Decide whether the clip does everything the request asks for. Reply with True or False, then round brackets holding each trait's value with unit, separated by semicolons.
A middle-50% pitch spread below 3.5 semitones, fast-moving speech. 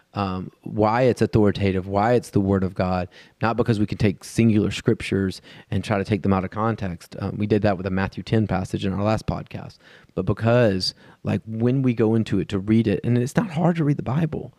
True (2.9 semitones; 235 wpm)